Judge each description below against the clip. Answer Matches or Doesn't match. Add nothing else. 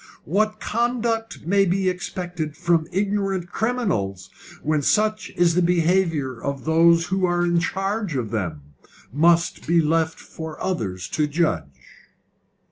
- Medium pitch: Matches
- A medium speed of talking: Doesn't match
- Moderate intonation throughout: Matches